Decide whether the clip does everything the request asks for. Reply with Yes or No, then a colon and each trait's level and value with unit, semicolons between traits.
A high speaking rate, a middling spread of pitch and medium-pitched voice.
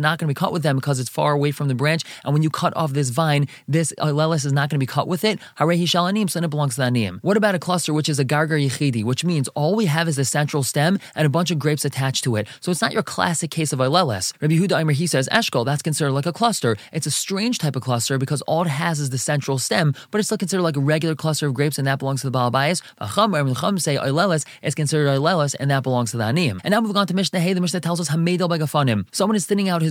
Yes: fast, 275 wpm; average, 3.9 semitones; medium, 155 Hz